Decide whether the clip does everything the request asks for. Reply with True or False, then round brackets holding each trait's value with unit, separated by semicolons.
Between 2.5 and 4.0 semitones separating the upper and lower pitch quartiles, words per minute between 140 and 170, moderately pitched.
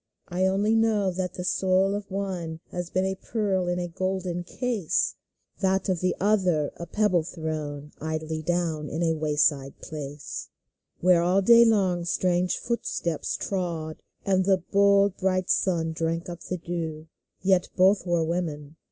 True (2.9 semitones; 160 wpm; 180 Hz)